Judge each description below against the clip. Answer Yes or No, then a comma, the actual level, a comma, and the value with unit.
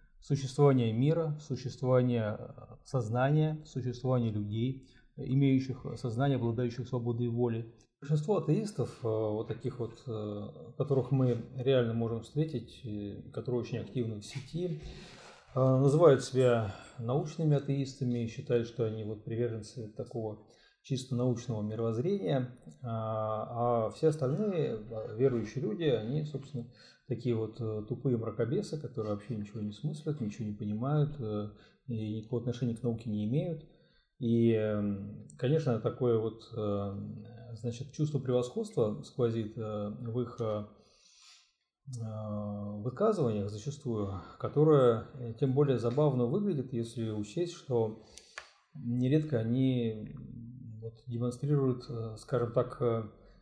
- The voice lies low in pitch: Yes, low, 120 Hz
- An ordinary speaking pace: No, slow, 100 wpm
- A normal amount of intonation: Yes, average, 3.2 semitones